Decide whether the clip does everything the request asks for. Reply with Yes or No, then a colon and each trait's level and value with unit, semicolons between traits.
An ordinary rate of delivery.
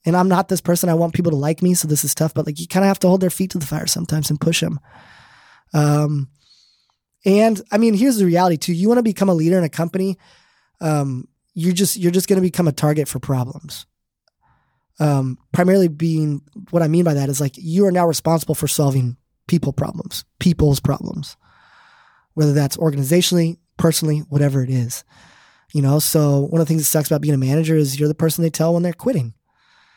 No: fast, 220 wpm